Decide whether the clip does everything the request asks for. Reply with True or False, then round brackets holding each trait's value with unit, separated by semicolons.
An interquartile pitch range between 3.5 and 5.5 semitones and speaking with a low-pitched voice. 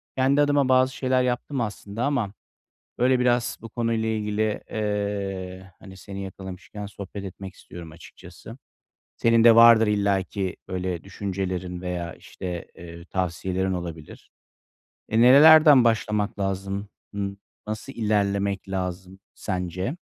True (3.8 semitones; 100 Hz)